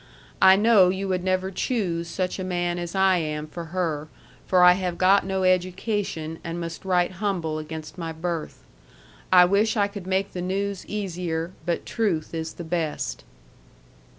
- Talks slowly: No, average, 170 wpm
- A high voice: No, medium, 180 Hz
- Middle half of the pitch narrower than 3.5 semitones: Yes, narrow, 2.4 semitones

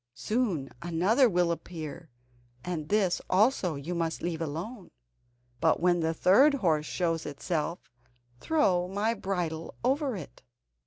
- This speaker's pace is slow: Yes, slow, 125 wpm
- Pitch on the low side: No, medium, 175 Hz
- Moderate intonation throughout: Yes, average, 4.3 semitones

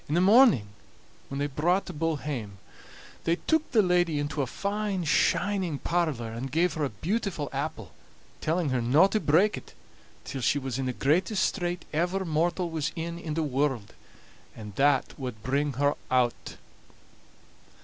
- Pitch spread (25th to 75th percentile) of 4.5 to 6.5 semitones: Yes, average, 4.8 semitones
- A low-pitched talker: No, medium, 155 Hz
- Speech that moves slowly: No, average, 170 wpm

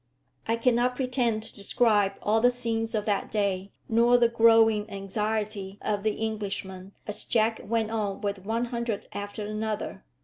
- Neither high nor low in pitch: No, high, 220 Hz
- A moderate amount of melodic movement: No, narrow, 2.1 semitones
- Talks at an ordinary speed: Yes, average, 160 wpm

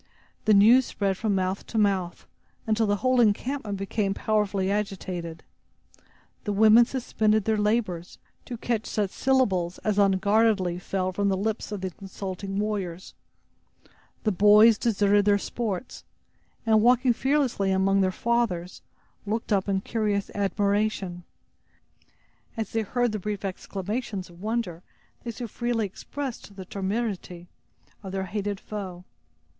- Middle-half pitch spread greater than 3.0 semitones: No, narrow, 2.5 semitones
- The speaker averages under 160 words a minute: Yes, slow, 135 wpm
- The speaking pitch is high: Yes, high, 205 Hz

